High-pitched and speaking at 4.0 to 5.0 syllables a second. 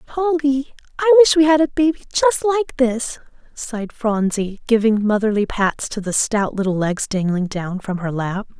Yes: high, 240 Hz; 4.7 syllables/s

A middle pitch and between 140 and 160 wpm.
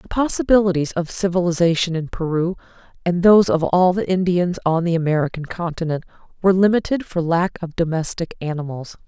Yes: medium, 175 Hz; average, 150 wpm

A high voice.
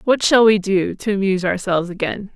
Yes: high, 195 Hz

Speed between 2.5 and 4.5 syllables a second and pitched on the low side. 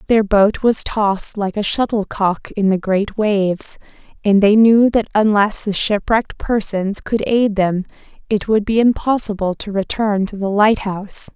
No: 4.4 syllables/s; high, 205 Hz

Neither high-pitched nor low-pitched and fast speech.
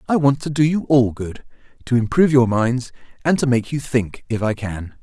No: low, 125 Hz; fast, 215 wpm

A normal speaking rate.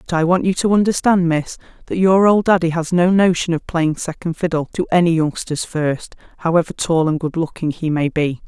No: fast, 210 wpm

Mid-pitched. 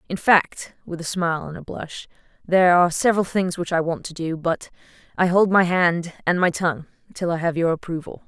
Yes: medium, 170 Hz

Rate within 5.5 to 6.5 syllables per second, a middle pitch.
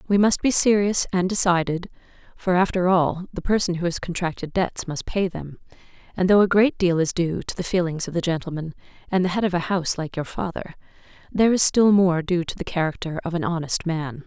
Yes: 5.7 syllables/s; medium, 175 Hz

